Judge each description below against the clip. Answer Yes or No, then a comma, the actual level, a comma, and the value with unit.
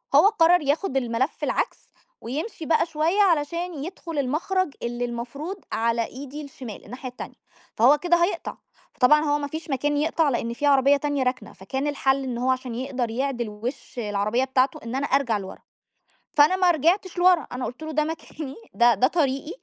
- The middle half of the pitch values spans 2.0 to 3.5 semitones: No, average, 4.0 semitones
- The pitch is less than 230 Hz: No, very high, 280 Hz